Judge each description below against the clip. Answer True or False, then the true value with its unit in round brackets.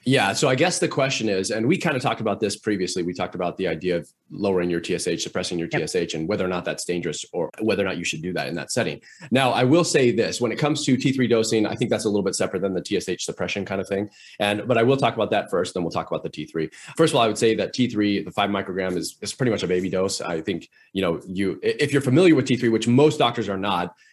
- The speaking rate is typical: False (290 wpm)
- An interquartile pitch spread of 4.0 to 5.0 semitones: True (4.6 semitones)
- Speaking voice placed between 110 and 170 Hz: False (100 Hz)